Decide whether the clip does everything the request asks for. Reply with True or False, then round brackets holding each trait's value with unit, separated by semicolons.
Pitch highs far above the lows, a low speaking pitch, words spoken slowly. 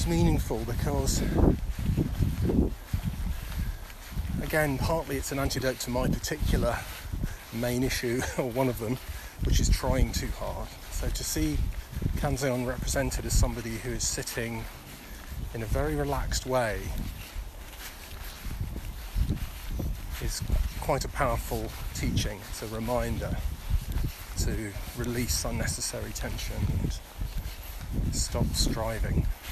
True (6.2 semitones; 105 Hz; 105 wpm)